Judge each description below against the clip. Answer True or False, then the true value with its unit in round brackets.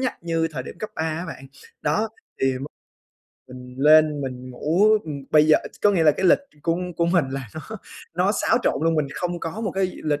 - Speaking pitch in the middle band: True (160 Hz)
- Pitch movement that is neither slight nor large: True (3.8 semitones)